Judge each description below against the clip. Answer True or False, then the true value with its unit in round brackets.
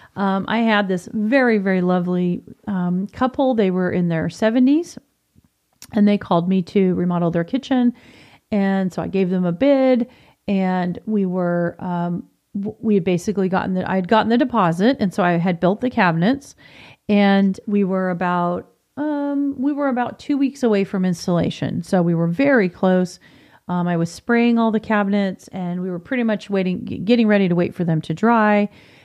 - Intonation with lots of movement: False (4.1 semitones)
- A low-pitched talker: False (195 Hz)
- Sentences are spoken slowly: False (185 wpm)